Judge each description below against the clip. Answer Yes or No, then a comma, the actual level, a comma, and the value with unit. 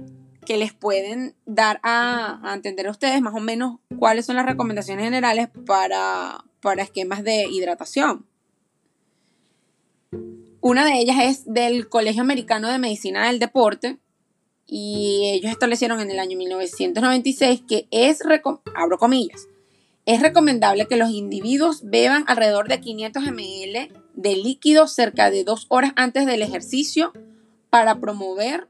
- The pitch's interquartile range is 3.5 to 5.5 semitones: Yes, average, 3.9 semitones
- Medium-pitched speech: No, high, 225 Hz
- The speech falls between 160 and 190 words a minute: No, average, 135 wpm